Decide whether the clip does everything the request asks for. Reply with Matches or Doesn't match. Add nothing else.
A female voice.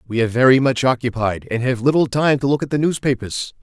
Doesn't match